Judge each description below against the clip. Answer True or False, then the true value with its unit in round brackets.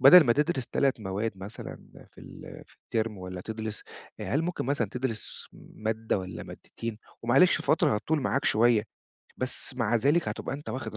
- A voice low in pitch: True (115 Hz)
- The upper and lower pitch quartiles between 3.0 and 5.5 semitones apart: True (4.1 semitones)